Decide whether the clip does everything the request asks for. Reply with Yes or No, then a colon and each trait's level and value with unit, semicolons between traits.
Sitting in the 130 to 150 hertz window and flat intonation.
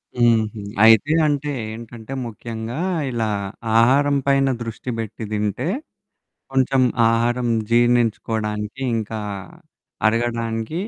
No: low, 115 Hz; narrow, 2.2 semitones